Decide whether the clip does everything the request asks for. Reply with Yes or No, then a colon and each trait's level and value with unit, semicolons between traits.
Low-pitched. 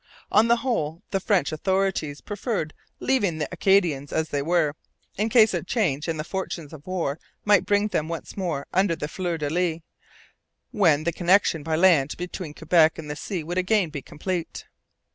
No: medium, 170 Hz